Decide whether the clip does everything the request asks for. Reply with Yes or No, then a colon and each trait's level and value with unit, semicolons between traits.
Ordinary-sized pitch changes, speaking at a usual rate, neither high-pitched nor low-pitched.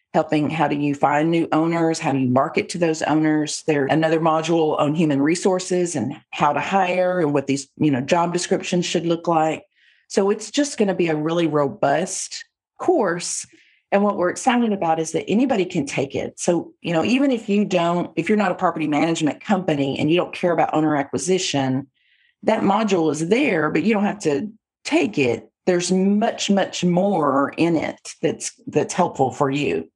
Yes: average, 4.4 semitones; average, 195 wpm; medium, 170 Hz